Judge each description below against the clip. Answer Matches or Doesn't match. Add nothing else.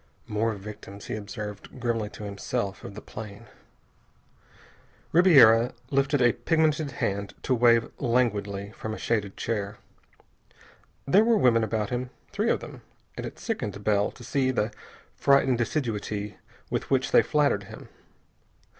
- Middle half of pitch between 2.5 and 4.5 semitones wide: Matches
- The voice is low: Matches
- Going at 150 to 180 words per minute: Doesn't match